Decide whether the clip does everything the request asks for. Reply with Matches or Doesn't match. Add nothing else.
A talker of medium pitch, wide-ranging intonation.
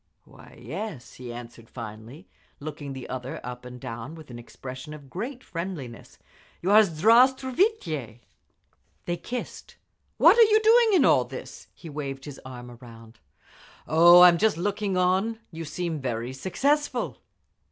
Matches